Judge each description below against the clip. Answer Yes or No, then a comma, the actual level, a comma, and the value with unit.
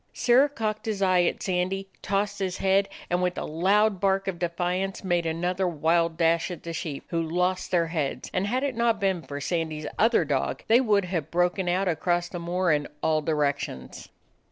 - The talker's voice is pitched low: No, medium, 180 Hz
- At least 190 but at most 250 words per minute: Yes, average, 195 wpm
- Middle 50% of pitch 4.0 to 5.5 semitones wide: No, average, 2.8 semitones